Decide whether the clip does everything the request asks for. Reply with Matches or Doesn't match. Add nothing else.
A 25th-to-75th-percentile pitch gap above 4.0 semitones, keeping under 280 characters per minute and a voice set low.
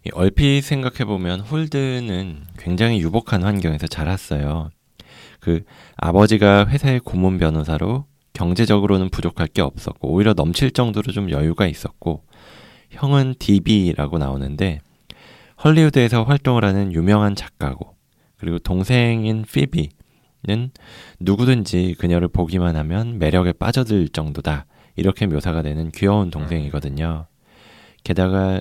Doesn't match